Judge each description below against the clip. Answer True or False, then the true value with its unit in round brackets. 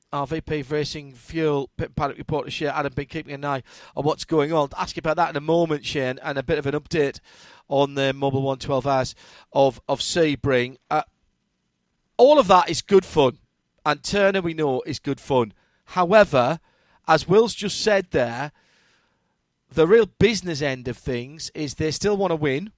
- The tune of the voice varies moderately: True (3.5 semitones)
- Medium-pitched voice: True (150 Hz)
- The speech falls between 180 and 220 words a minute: True (190 wpm)